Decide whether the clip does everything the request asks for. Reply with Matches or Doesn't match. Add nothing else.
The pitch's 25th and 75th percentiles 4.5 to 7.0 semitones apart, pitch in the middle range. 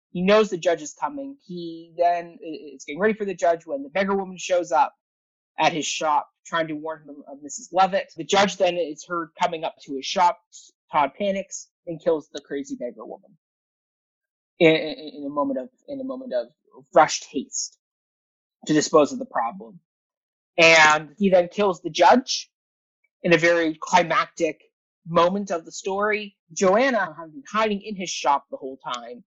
Matches